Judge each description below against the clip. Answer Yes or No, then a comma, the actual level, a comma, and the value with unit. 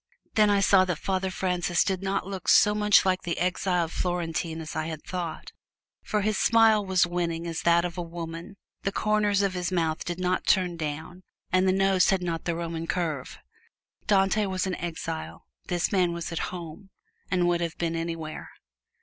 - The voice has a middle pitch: Yes, medium, 180 Hz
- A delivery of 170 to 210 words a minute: Yes, average, 190 wpm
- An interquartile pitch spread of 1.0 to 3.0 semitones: Yes, narrow, 2.4 semitones